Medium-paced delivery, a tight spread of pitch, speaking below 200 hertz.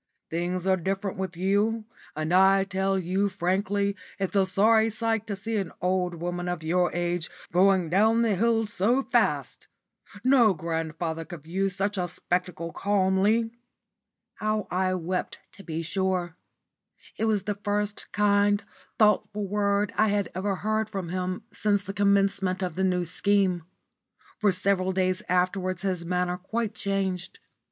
Yes: average, 150 wpm; narrow, 2.2 semitones; high, 190 Hz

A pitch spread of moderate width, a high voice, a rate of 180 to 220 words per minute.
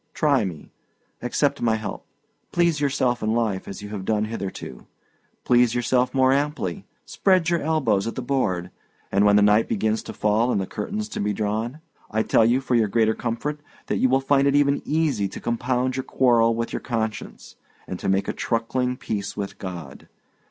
No: average, 4.2 semitones; low, 115 Hz; average, 195 wpm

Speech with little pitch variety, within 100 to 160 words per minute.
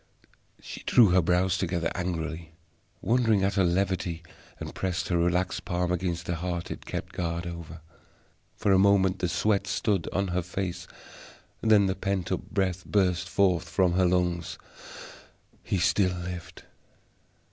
Yes: narrow, 1.9 semitones; average, 145 wpm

